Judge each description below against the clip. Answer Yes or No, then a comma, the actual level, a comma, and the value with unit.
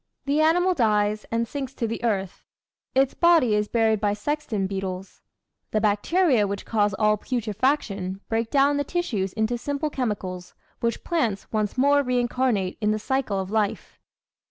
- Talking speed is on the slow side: No, average, 155 wpm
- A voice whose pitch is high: Yes, high, 225 Hz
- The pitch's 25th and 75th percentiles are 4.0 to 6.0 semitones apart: Yes, average, 4.8 semitones